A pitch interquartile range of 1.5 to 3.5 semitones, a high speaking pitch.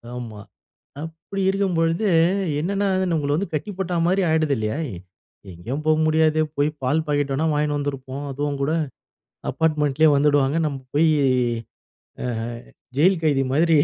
No: narrow, 2.5 semitones; medium, 155 Hz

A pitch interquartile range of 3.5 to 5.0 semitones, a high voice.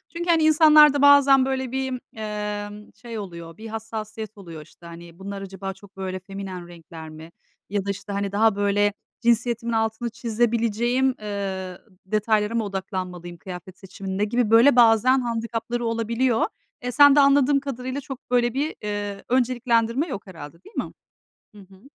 Yes: average, 4.1 semitones; high, 220 Hz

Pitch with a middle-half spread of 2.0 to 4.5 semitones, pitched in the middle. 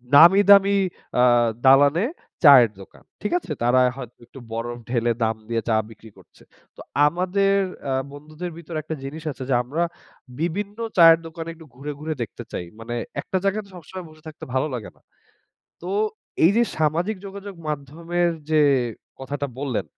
No: average, 4.9 semitones; medium, 155 Hz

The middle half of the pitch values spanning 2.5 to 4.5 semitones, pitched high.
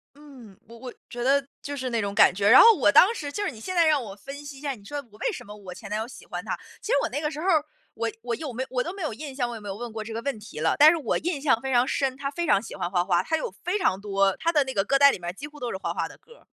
No: wide, 5.6 semitones; very high, 260 Hz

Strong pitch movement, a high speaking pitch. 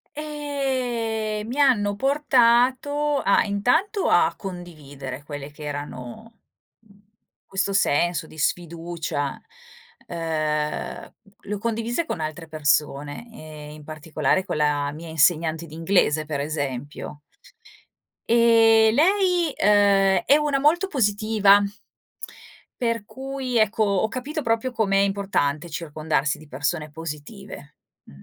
Yes: wide, 7.3 semitones; high, 195 Hz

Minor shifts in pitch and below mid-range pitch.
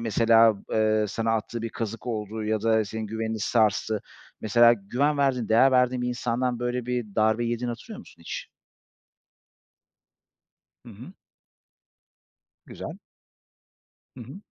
Yes: narrow, 2.0 semitones; low, 115 Hz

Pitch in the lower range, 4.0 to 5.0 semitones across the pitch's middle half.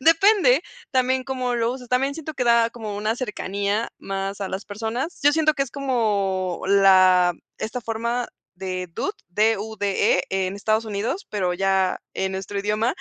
No: high, 215 Hz; average, 4.5 semitones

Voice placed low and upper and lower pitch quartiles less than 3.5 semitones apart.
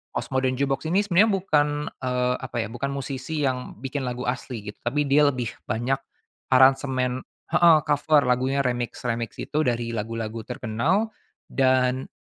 Yes: low, 130 Hz; average, 2.8 semitones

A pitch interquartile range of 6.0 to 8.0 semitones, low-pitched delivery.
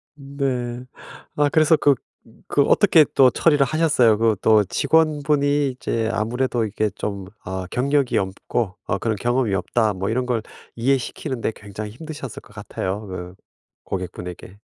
No: average, 5.2 semitones; low, 120 Hz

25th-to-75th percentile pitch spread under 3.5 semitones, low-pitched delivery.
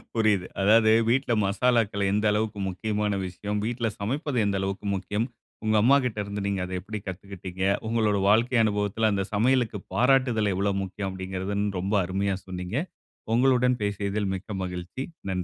Yes: narrow, 2.6 semitones; low, 105 Hz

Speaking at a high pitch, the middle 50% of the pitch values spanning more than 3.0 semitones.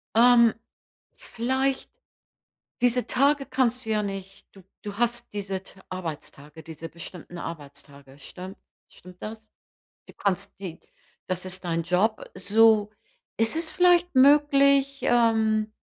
Yes: high, 215 Hz; average, 5.2 semitones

